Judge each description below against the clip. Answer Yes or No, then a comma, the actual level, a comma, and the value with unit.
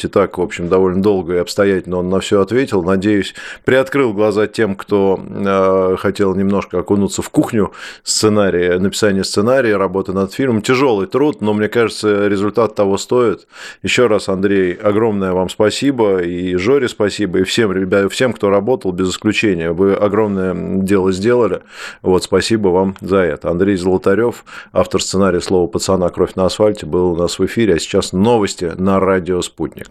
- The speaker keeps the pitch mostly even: Yes, narrow, 2.1 semitones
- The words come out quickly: Yes, fast, 165 wpm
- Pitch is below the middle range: Yes, very low, 95 Hz